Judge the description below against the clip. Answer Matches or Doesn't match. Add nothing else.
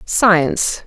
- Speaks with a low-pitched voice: Doesn't match